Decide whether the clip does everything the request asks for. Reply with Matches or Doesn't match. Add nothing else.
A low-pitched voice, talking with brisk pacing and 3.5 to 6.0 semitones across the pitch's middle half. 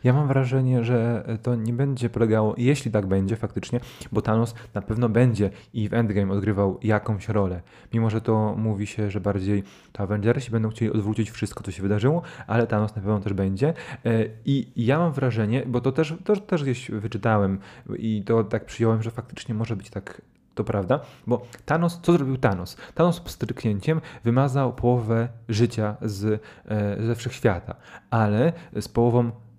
Doesn't match